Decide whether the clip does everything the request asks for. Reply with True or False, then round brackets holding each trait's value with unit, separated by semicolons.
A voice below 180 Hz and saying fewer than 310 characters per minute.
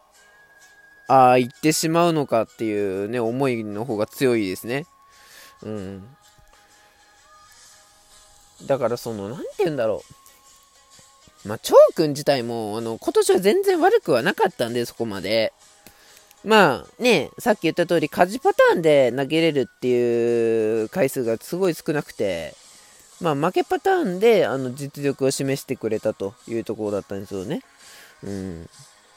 True (135 Hz; 285 characters per minute)